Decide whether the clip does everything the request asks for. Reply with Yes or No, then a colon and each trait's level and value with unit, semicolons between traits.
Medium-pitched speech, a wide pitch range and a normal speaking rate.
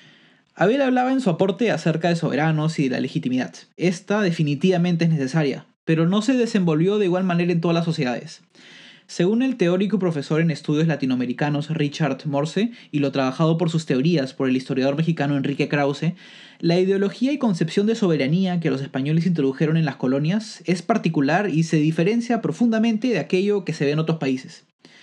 No: medium, 165 Hz; average, 4.9 semitones; average, 180 wpm